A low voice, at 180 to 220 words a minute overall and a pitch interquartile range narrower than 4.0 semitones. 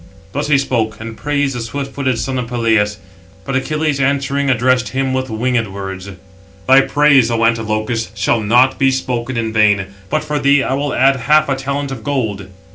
Yes: low, 130 Hz; average, 185 wpm; average, 3.5 semitones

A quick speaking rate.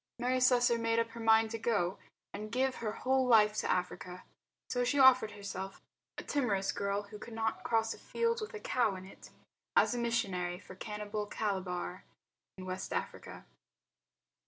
No: average, 180 wpm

